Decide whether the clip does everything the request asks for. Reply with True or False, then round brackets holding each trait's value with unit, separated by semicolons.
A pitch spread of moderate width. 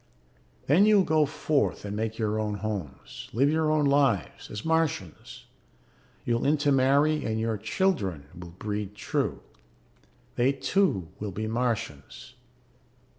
False (6.2 semitones)